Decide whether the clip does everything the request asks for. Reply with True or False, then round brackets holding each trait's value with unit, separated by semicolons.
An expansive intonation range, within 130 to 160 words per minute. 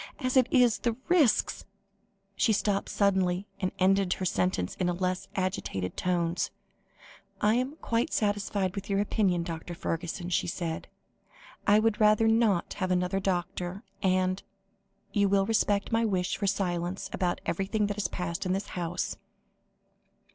False (2.6 semitones; 145 wpm)